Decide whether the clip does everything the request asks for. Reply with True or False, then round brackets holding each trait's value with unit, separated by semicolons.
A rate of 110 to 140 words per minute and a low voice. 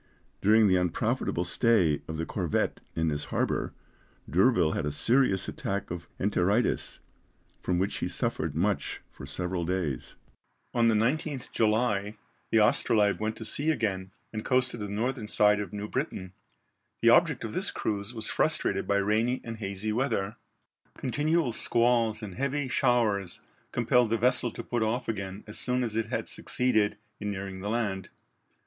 False (160 wpm; 110 Hz)